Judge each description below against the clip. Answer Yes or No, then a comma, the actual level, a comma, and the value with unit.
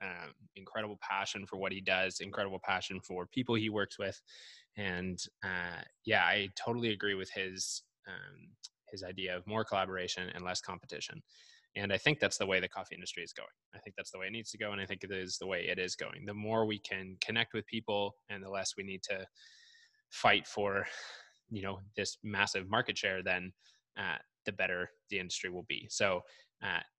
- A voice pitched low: Yes, very low, 95 Hz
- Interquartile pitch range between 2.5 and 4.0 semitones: Yes, average, 2.9 semitones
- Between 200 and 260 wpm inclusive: Yes, fast, 205 wpm